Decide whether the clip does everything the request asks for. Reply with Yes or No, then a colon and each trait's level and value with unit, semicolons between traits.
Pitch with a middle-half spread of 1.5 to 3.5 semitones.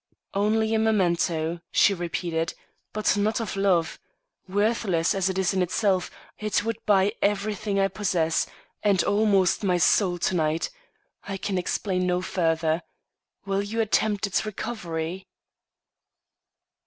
Yes: average, 2.9 semitones